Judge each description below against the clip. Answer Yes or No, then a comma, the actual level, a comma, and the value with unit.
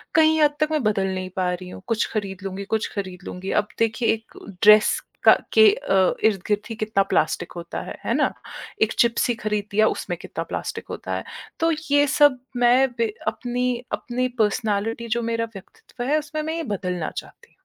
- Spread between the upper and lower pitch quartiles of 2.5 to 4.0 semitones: No, average, 4.6 semitones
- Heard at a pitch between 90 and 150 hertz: No, high, 220 Hz